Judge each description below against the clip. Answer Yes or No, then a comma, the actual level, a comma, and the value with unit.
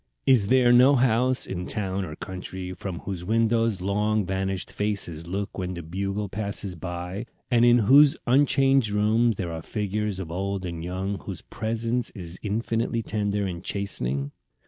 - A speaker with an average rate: Yes, average, 160 wpm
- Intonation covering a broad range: No, average, 3.7 semitones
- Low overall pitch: Yes, low, 100 Hz